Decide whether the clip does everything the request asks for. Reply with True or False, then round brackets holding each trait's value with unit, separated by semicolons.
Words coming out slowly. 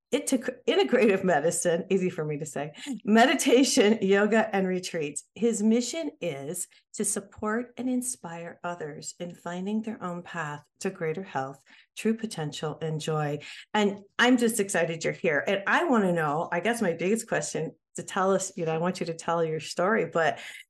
False (180 wpm)